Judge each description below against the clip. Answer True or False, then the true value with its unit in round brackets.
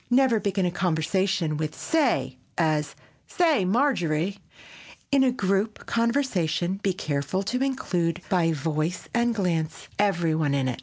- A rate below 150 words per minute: True (140 wpm)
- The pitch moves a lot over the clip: True (6.3 semitones)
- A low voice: False (185 Hz)